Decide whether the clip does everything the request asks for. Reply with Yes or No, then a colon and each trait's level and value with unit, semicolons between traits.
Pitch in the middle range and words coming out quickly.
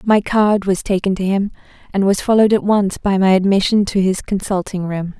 No: high, 195 Hz; fast, 210 wpm